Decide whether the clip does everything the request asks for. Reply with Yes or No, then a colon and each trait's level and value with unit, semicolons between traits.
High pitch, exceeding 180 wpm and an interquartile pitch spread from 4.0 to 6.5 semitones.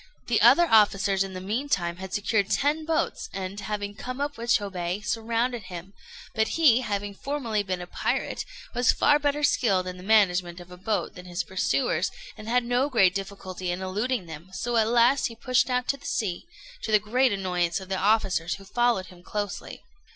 Yes: high, 205 Hz; average, 195 wpm; average, 4.6 semitones